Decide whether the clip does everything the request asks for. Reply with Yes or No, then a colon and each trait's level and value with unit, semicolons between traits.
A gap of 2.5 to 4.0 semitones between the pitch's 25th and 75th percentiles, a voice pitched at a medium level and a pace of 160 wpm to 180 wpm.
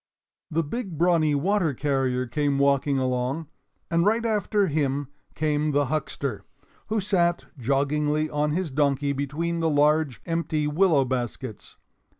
No: average, 3.2 semitones; medium, 150 Hz; slow, 135 wpm